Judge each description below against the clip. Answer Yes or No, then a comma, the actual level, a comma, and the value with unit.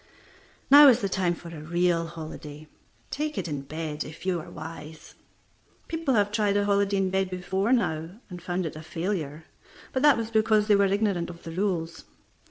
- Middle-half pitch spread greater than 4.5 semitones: No, average, 4.1 semitones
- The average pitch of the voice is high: No, medium, 180 Hz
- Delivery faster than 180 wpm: Yes, average, 190 wpm